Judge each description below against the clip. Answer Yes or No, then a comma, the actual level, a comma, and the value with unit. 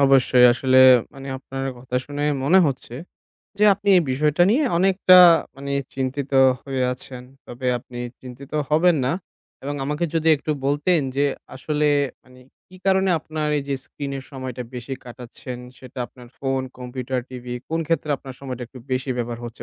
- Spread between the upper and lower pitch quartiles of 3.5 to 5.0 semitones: No, average, 2.9 semitones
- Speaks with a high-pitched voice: No, low, 135 Hz